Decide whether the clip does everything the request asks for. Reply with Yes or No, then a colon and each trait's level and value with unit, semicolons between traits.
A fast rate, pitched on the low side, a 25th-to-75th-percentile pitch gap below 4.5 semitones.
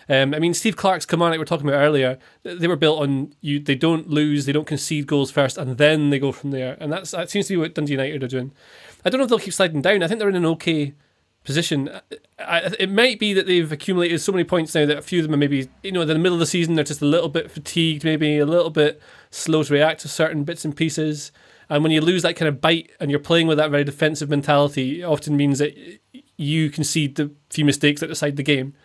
No: fast, 270 wpm; medium, 155 Hz; average, 2.7 semitones